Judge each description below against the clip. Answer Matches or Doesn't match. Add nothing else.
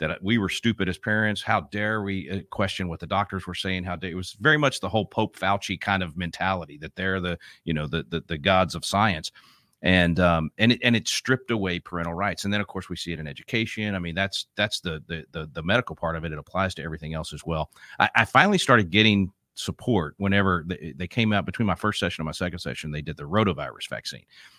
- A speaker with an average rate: Doesn't match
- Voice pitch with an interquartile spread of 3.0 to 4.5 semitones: Matches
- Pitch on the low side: Matches